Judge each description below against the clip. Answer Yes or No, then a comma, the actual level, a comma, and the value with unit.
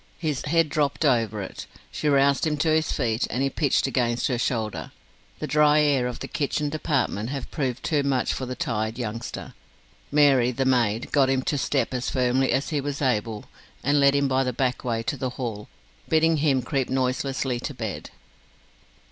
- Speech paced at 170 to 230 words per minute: Yes, average, 190 wpm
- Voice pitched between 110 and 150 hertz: Yes, low, 135 Hz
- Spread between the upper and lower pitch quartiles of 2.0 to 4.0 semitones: Yes, average, 2.9 semitones